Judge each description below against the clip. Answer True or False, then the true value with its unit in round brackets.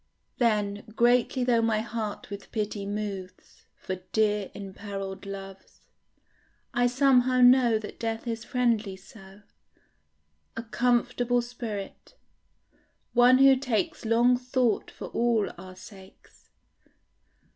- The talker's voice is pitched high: True (225 Hz)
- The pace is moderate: False (110 wpm)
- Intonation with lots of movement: False (3.3 semitones)